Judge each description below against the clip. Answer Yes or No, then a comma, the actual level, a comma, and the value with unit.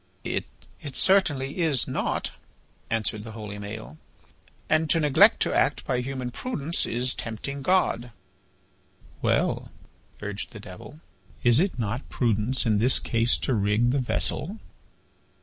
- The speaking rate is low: Yes, slow, 130 wpm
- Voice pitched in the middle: No, low, 125 Hz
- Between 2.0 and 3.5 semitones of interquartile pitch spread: No, average, 4.7 semitones